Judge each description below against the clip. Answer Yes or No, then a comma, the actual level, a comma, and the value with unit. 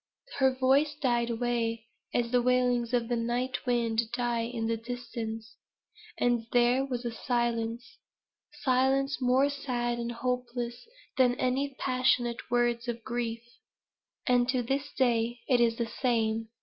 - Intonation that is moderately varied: No, narrow, 1.4 semitones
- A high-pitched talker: Yes, high, 240 Hz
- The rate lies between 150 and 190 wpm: No, slow, 135 wpm